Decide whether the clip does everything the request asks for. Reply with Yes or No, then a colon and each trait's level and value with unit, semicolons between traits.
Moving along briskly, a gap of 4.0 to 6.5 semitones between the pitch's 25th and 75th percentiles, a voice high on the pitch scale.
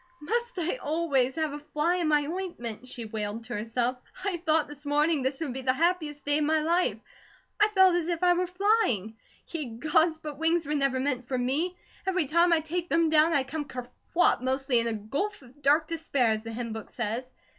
Yes: fast, 215 wpm; average, 4.9 semitones; very high, 295 Hz